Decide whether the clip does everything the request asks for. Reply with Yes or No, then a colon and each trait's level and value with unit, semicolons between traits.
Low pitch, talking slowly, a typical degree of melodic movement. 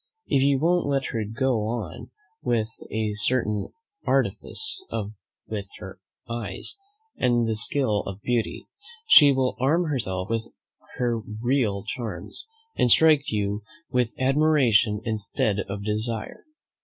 Yes: low, 115 Hz; slow, 125 wpm; average, 4.0 semitones